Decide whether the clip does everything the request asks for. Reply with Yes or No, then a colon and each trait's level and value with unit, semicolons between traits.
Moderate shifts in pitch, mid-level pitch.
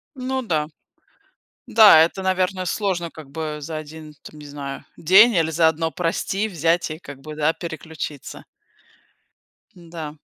Yes: average, 3.2 semitones; medium, 160 Hz